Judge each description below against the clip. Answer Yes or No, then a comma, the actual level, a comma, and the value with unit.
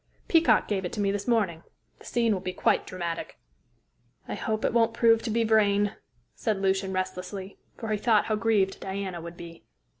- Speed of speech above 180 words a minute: Yes, average, 190 wpm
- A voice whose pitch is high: Yes, high, 200 Hz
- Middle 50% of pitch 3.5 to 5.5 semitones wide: No, average, 2.9 semitones